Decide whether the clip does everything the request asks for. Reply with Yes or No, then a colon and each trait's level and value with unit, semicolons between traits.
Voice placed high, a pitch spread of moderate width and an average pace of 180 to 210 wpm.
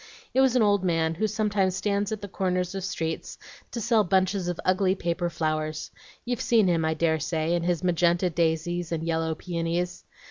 No: medium, 175 Hz; average, 3.2 semitones; average, 190 wpm